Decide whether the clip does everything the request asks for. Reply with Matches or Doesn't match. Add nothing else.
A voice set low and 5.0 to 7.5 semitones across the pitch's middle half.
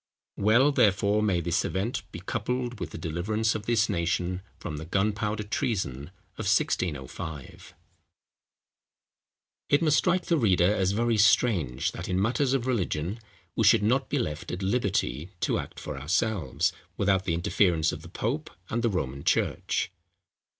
Matches